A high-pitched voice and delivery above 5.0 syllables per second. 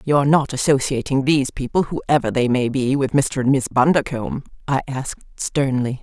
No: low, 130 Hz; 5.3 syllables/s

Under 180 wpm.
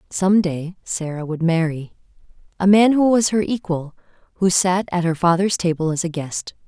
Yes: average, 170 wpm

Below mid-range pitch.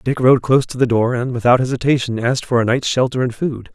Yes: low, 125 Hz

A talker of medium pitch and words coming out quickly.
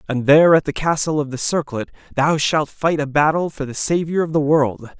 Yes: medium, 150 Hz; fast, 230 wpm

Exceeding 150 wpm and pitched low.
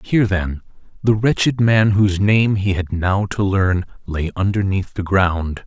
Yes: average, 170 wpm; low, 100 Hz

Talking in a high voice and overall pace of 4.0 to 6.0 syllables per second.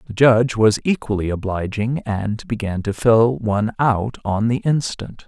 No: low, 110 Hz; 4.5 syllables/s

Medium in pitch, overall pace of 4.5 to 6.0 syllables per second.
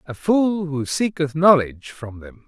No: medium, 150 Hz; 4.3 syllables/s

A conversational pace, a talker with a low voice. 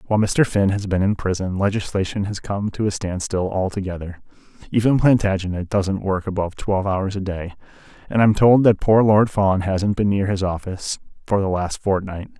Yes: average, 190 wpm; low, 100 Hz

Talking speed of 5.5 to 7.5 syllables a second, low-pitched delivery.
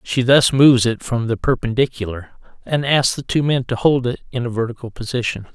Yes: 5.6 syllables/s; low, 125 Hz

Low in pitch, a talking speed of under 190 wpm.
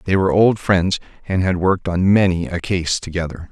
No: very low, 90 Hz; fast, 205 wpm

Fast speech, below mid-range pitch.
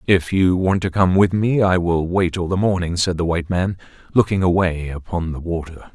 Yes: fast, 220 wpm; very low, 90 Hz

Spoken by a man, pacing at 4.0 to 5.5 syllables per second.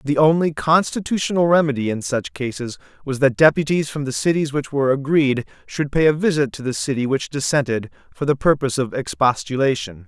No: male; 5.7 syllables/s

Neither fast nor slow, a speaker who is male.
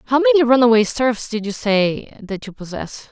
No: average, 190 wpm; female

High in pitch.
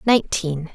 No: medium, 180 Hz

